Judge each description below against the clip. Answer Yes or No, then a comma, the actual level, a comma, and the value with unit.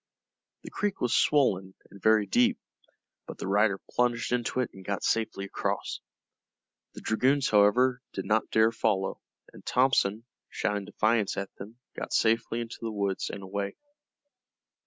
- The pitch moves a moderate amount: Yes, average, 3.2 semitones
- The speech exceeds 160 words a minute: No, average, 150 wpm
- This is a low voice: Yes, low, 110 Hz